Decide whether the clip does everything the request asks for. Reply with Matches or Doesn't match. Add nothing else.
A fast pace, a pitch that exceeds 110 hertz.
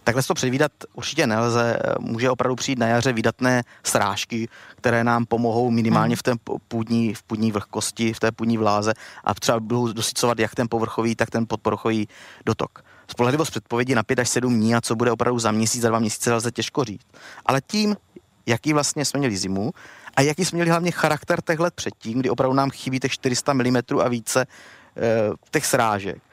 Matches